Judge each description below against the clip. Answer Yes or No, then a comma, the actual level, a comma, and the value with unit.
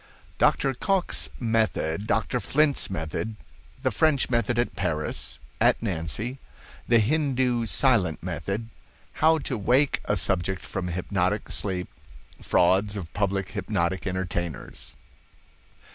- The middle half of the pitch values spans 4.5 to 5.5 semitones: Yes, average, 5.1 semitones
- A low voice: Yes, low, 105 Hz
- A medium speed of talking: No, slow, 90 wpm